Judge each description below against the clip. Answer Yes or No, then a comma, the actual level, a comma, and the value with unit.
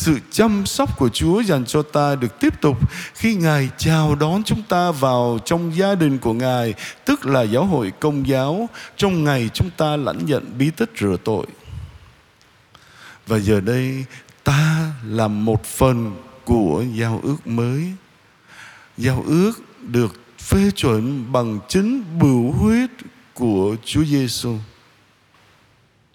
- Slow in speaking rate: Yes, slow, 145 wpm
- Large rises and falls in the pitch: Yes, wide, 6.2 semitones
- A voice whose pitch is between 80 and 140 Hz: Yes, low, 135 Hz